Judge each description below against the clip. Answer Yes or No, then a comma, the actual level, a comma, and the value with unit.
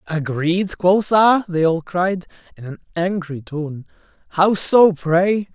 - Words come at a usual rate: No, slow, 130 wpm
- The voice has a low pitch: No, medium, 175 Hz